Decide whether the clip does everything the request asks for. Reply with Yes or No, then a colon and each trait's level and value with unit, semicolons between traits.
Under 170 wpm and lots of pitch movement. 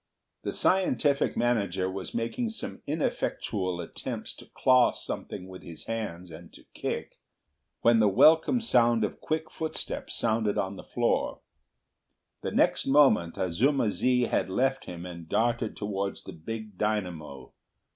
Yes: average, 140 wpm; wide, 5.7 semitones